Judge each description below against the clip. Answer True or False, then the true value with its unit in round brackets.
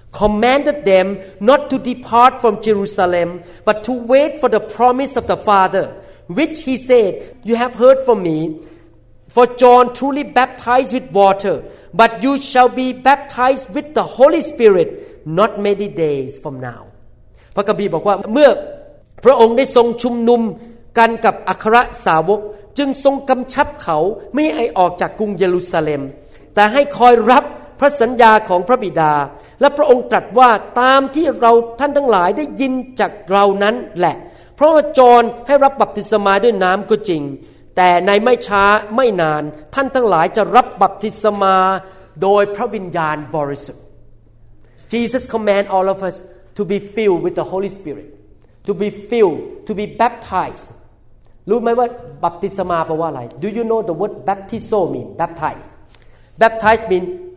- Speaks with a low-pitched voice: False (210 Hz)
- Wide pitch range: True (5.8 semitones)